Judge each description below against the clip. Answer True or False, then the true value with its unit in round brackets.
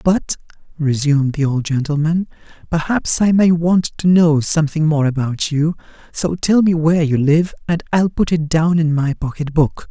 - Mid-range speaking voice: True (160 Hz)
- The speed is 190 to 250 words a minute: False (180 wpm)